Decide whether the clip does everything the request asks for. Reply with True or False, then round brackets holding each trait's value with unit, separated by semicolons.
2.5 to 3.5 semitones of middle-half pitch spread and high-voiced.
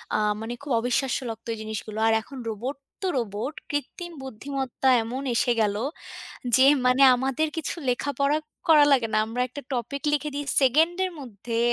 False (3.9 semitones; 260 Hz)